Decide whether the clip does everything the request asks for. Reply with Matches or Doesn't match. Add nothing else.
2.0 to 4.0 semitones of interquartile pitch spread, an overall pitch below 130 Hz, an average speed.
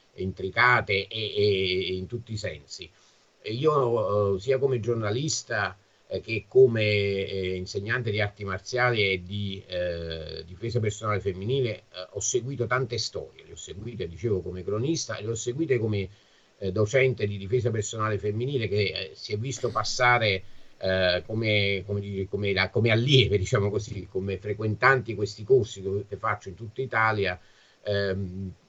Matches